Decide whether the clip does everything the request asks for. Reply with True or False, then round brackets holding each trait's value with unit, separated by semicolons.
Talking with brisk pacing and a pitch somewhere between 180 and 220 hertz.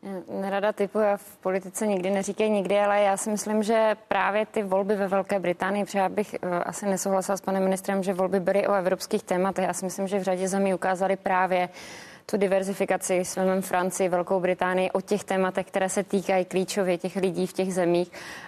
True (195 wpm; 190 Hz)